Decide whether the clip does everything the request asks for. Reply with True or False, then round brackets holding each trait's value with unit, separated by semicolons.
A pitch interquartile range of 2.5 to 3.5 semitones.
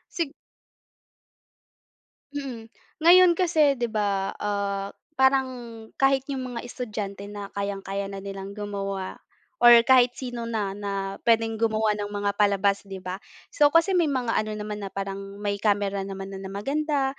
False (4.6 semitones)